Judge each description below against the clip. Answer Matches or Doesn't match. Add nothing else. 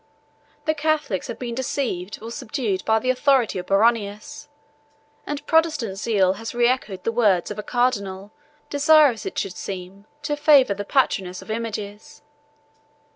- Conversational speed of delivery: Matches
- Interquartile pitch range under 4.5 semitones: Doesn't match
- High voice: Matches